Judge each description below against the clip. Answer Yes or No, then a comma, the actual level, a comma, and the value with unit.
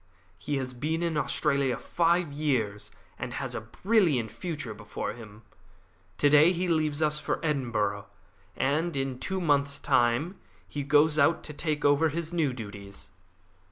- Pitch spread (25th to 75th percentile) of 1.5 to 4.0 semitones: No, average, 4.7 semitones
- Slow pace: No, average, 155 wpm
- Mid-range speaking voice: Yes, medium, 145 Hz